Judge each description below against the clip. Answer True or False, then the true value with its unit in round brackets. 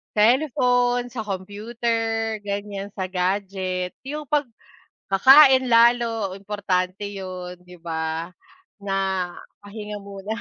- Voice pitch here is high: True (205 Hz)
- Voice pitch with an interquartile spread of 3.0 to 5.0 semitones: True (3.7 semitones)